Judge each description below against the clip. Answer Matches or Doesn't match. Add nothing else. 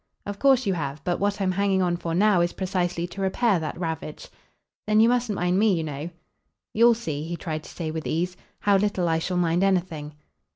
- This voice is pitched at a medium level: Matches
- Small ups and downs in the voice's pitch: Doesn't match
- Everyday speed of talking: Doesn't match